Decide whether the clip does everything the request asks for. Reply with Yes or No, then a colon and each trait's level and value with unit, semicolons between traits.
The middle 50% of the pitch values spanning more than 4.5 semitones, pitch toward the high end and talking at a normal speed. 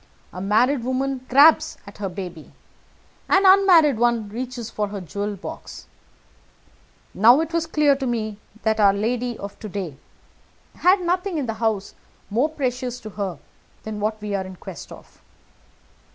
Yes: wide, 5.4 semitones; high, 230 Hz; average, 160 wpm